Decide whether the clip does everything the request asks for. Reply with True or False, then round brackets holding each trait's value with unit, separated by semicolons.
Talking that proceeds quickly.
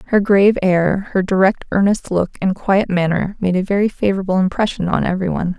False (195 wpm)